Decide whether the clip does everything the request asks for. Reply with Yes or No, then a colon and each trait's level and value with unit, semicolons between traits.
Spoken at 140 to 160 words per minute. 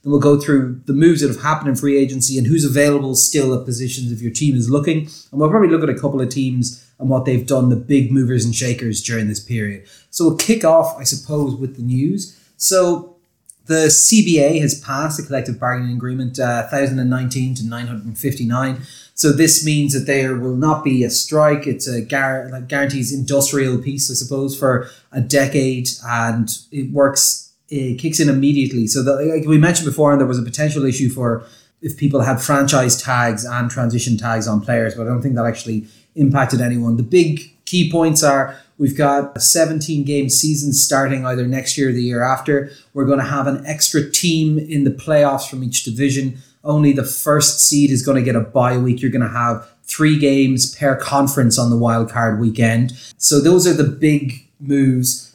No: average, 200 wpm